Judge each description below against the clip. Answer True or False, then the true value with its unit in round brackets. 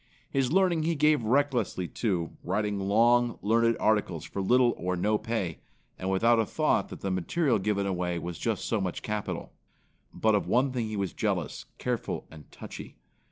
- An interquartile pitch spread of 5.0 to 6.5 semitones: False (4.3 semitones)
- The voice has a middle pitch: False (110 Hz)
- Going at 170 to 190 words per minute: True (175 wpm)